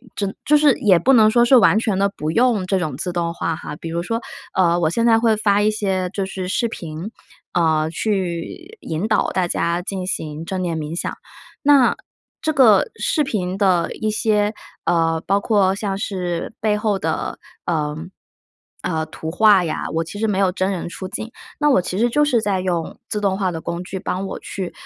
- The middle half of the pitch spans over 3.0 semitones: Yes, average, 4.0 semitones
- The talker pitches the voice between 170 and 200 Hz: Yes, high, 190 Hz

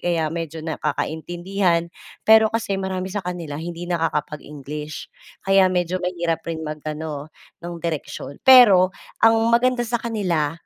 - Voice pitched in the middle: Yes, medium, 170 Hz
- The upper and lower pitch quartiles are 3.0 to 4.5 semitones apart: Yes, average, 3.6 semitones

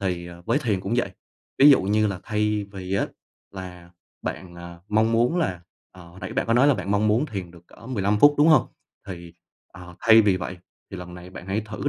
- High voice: No, low, 100 Hz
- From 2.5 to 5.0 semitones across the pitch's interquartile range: Yes, average, 3.8 semitones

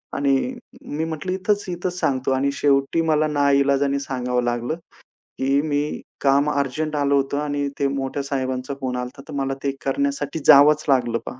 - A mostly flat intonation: Yes, narrow, 1.9 semitones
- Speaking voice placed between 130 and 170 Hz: Yes, medium, 140 Hz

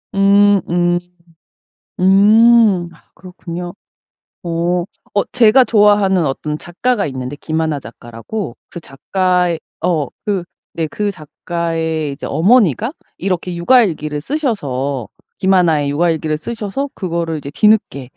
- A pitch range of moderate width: Yes, average, 4.6 semitones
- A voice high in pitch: No, medium, 175 Hz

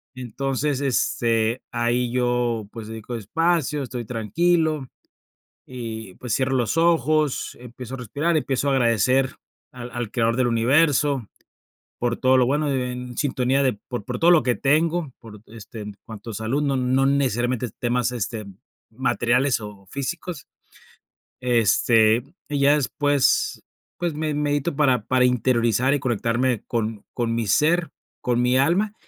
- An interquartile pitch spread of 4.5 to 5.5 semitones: No, average, 3.3 semitones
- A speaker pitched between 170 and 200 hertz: No, low, 125 Hz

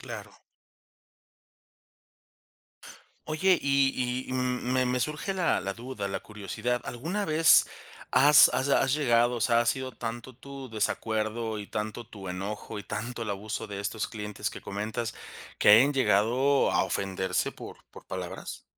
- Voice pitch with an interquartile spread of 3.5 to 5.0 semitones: Yes, average, 3.9 semitones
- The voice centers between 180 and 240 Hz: No, low, 120 Hz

